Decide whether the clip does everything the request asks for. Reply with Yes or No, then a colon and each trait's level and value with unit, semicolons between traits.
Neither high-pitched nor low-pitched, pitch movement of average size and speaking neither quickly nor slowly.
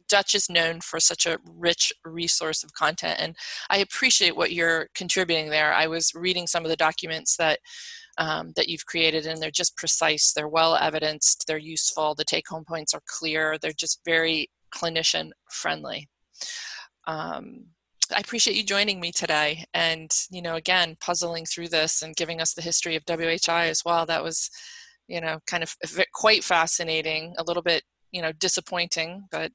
No: medium, 165 Hz; narrow, 1.6 semitones; average, 175 wpm